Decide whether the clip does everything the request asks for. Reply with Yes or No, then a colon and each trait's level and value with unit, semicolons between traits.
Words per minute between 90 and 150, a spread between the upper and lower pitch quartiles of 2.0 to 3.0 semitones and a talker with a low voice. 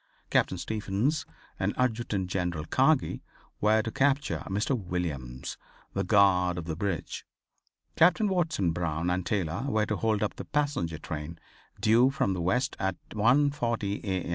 No: average, 145 wpm; wide, 5.6 semitones; low, 100 Hz